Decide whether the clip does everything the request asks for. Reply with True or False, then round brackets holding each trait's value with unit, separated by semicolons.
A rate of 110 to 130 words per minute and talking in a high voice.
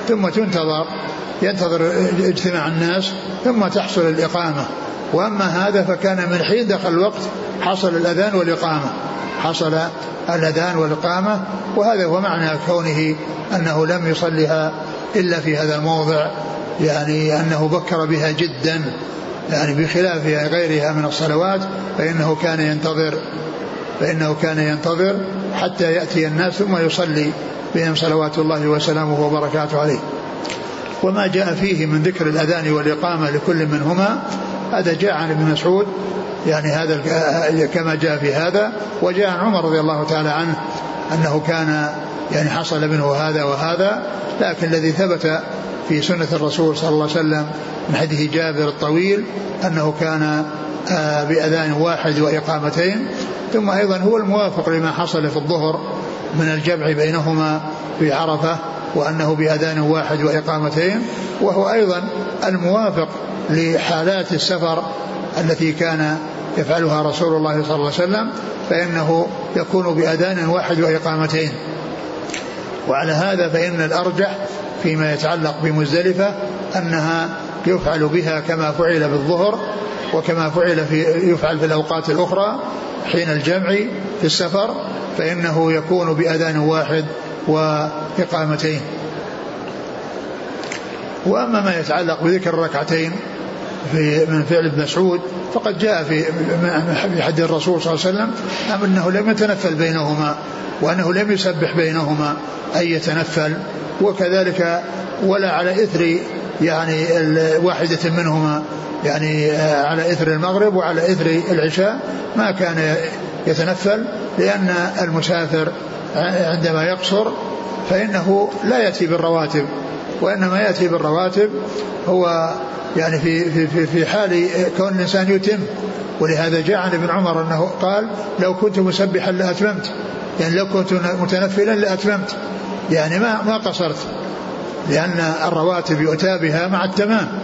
False (115 wpm; 165 Hz)